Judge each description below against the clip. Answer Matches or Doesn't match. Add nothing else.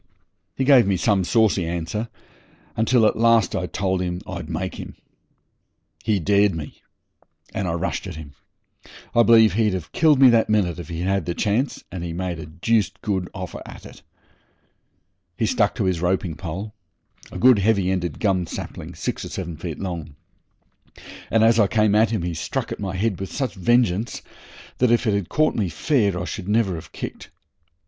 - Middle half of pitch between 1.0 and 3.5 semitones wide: Doesn't match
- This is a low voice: Matches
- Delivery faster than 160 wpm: Matches